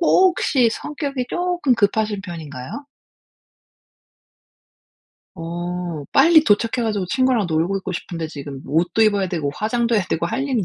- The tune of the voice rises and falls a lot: Yes, wide, 7.0 semitones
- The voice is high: Yes, high, 205 Hz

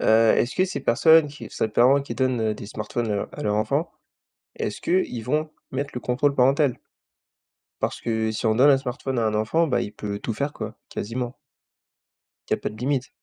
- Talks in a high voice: No, low, 125 Hz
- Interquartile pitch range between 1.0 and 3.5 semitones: No, average, 4.2 semitones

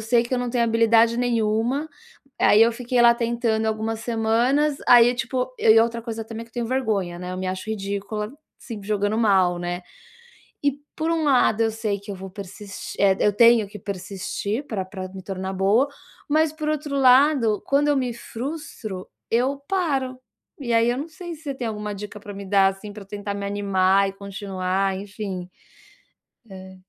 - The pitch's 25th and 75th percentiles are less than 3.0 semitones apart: No, average, 3.8 semitones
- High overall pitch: Yes, high, 220 Hz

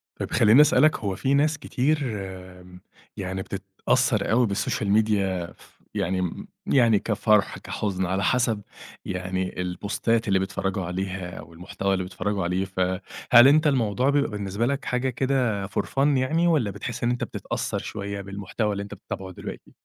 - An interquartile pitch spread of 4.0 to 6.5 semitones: Yes, average, 4.5 semitones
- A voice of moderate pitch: No, low, 100 Hz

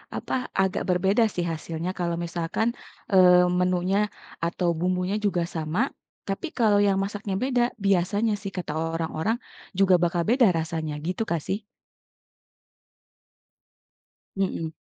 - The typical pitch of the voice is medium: Yes, medium, 180 Hz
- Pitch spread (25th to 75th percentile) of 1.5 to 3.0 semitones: Yes, average, 2.7 semitones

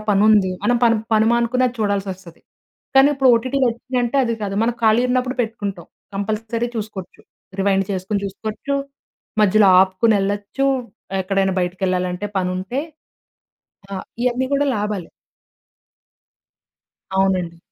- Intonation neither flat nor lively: Yes, average, 3.7 semitones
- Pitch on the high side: Yes, high, 210 Hz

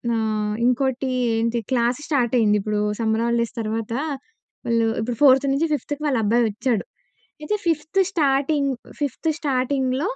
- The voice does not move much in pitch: No, average, 3.6 semitones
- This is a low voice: No, very high, 250 Hz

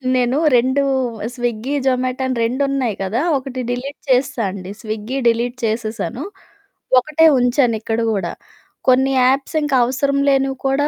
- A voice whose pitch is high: Yes, very high, 255 Hz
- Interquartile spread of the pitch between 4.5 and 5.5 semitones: No, average, 2.7 semitones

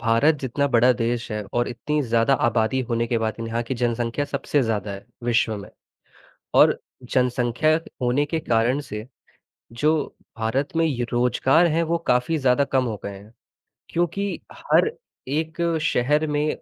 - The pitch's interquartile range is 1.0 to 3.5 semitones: No, average, 4.2 semitones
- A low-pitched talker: Yes, low, 125 Hz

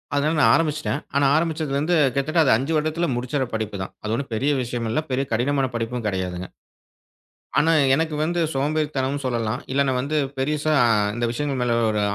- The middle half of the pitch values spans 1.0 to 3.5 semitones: No, average, 4.2 semitones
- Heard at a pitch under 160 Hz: Yes, medium, 140 Hz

